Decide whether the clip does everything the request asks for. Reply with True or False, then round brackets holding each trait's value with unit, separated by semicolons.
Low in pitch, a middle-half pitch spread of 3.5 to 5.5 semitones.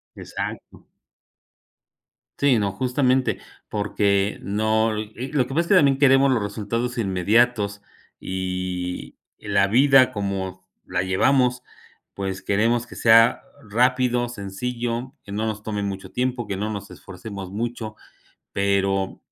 True (110 Hz; 3.9 semitones)